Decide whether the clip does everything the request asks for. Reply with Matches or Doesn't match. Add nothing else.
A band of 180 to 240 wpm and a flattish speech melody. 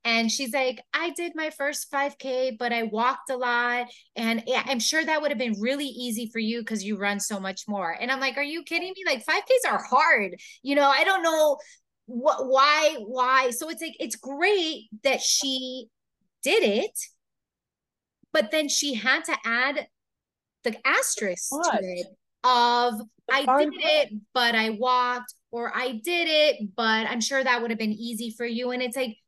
Doesn't match